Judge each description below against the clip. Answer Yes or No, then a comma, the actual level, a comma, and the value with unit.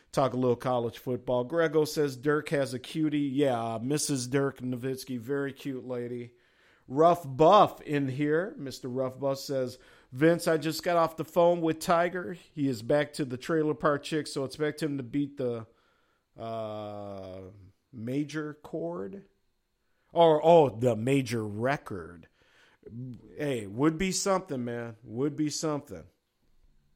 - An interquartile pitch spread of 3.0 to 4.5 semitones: Yes, average, 4.0 semitones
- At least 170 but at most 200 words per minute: No, average, 145 wpm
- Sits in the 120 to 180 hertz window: Yes, medium, 140 Hz